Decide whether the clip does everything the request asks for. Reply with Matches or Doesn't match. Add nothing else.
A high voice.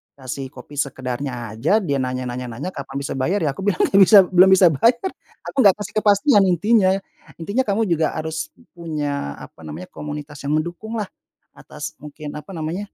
Doesn't match